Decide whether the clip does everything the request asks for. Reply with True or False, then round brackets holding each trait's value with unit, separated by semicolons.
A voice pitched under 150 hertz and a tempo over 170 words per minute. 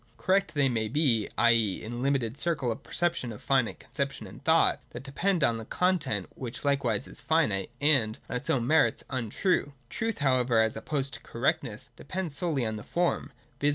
True (135 Hz; 190 wpm)